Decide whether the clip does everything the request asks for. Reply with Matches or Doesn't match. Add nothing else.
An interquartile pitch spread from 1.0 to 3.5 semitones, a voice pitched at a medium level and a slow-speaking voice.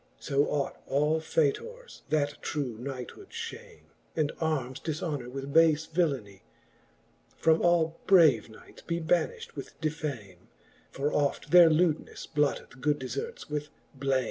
Matches